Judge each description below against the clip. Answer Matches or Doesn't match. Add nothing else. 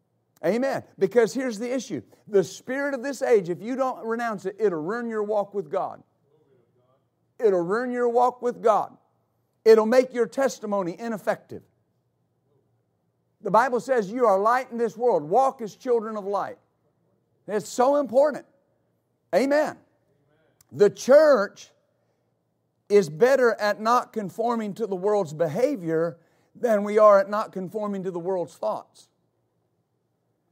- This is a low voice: Doesn't match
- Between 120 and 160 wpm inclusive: Matches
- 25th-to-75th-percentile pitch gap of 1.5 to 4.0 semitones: Doesn't match